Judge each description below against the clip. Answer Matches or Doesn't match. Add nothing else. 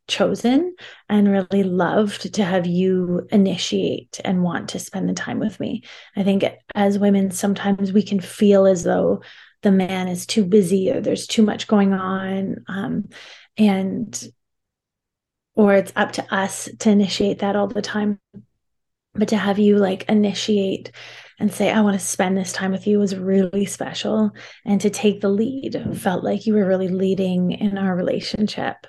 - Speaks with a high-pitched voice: Matches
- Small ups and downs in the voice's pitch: Matches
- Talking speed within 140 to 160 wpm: Doesn't match